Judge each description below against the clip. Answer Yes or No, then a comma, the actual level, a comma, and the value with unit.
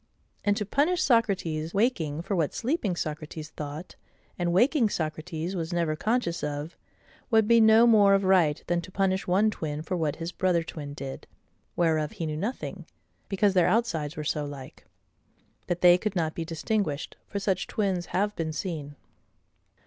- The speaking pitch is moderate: Yes, medium, 175 Hz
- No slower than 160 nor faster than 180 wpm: Yes, average, 170 wpm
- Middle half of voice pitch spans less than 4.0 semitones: No, average, 4.7 semitones